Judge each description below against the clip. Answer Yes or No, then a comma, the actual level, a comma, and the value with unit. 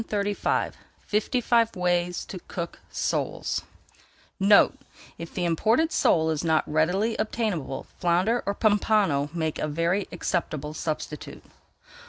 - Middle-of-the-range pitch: Yes, medium, 180 Hz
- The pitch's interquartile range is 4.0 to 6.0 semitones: Yes, average, 4.8 semitones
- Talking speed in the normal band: No, slow, 125 wpm